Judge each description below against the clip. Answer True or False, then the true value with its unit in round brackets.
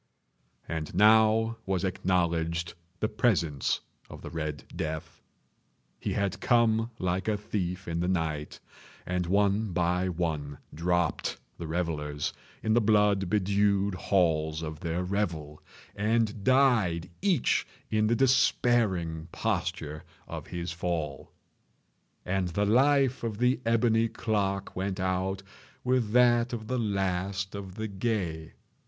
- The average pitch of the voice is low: True (95 Hz)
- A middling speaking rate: False (125 wpm)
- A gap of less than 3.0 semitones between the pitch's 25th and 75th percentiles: False (4.4 semitones)